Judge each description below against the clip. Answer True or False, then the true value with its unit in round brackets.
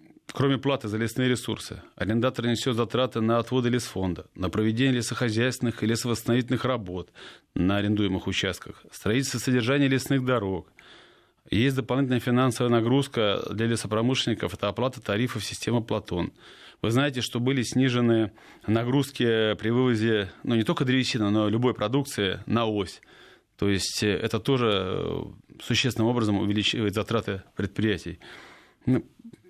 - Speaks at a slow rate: False (125 wpm)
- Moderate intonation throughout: True (3.2 semitones)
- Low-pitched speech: True (115 Hz)